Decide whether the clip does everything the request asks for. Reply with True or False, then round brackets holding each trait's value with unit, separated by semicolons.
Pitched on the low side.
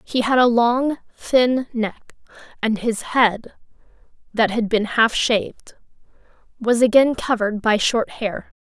False (230 Hz)